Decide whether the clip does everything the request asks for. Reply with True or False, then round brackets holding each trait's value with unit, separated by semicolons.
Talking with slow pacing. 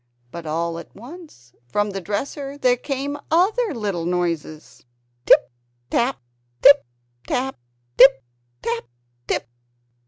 True (115 wpm)